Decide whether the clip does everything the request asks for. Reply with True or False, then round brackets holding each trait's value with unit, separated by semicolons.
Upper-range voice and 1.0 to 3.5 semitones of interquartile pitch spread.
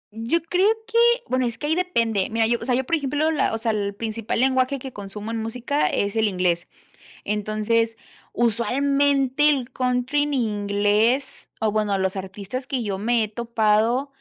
False (235 Hz; 4.1 semitones)